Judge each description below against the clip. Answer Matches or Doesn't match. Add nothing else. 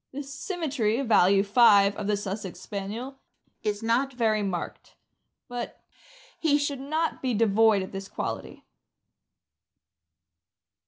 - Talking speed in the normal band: Doesn't match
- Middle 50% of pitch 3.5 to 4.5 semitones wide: Doesn't match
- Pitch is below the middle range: Doesn't match